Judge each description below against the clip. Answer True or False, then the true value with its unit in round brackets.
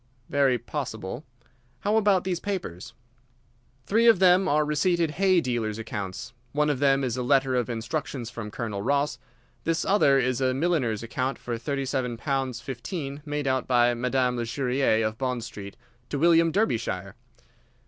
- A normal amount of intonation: True (4.2 semitones)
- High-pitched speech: False (135 Hz)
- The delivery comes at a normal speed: True (160 wpm)